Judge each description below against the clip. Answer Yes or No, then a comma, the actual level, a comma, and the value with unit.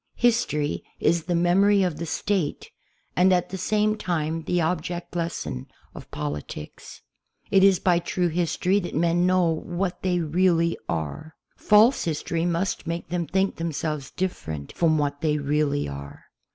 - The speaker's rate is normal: Yes, average, 150 wpm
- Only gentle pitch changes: No, average, 3.2 semitones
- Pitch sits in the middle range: Yes, medium, 170 Hz